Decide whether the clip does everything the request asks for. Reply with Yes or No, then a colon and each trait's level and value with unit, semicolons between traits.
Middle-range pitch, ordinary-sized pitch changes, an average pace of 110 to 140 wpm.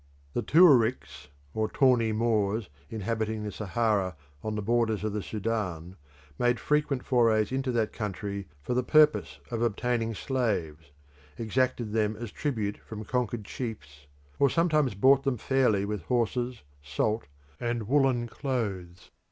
No: low, 115 Hz; average, 3.2 semitones; slow, 135 wpm